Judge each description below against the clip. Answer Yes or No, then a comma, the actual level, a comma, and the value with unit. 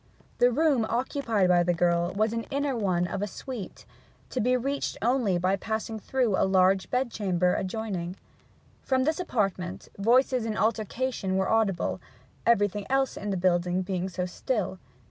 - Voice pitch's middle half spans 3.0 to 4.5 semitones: No, average, 5.0 semitones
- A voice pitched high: Yes, high, 210 Hz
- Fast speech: No, average, 160 wpm